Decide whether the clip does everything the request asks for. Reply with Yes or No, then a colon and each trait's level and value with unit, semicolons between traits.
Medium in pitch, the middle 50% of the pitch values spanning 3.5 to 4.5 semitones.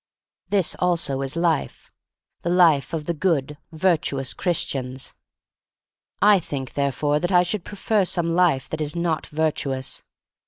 Yes: medium, 160 Hz; average, 4.0 semitones